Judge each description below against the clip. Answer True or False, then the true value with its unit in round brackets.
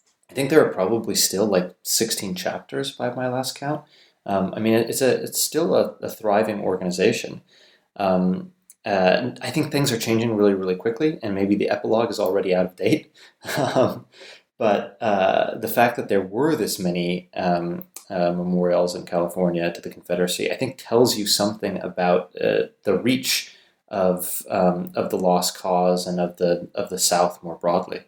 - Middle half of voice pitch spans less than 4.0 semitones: False (4.3 semitones)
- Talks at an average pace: True (175 wpm)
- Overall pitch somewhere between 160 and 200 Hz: False (95 Hz)